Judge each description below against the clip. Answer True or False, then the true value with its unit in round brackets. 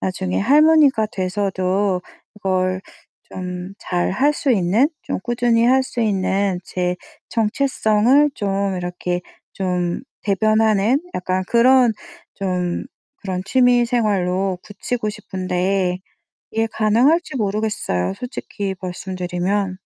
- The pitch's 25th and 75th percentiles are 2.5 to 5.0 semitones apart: True (4.0 semitones)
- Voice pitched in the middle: False (200 Hz)